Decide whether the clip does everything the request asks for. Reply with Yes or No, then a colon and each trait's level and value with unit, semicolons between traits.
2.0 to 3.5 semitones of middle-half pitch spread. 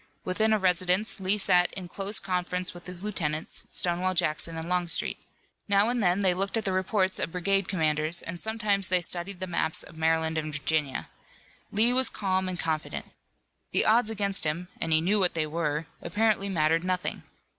Yes: average, 3.2 semitones